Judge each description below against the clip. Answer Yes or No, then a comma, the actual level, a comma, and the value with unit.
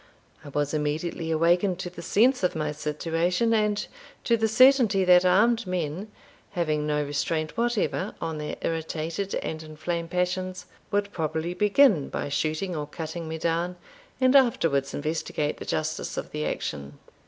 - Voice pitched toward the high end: No, medium, 170 Hz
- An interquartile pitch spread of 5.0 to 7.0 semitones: No, average, 4.3 semitones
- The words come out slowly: No, average, 155 wpm